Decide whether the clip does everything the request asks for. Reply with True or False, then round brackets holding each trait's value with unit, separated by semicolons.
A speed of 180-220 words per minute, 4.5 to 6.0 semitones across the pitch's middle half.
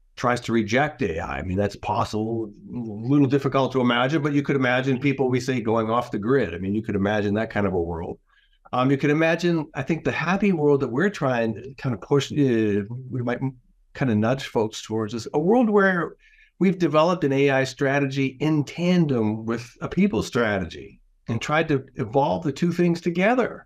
True (205 wpm; 4.9 semitones)